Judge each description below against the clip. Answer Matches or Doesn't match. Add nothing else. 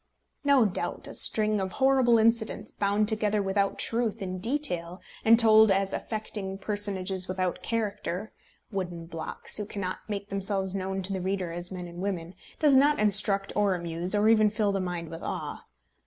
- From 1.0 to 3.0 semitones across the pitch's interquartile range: Matches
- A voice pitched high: Matches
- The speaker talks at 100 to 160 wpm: Doesn't match